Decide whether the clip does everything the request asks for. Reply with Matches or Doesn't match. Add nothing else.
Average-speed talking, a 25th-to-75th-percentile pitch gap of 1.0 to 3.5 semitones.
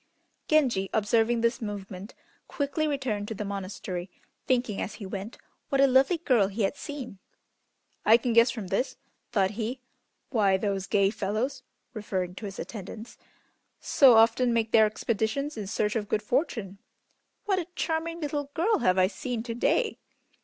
Doesn't match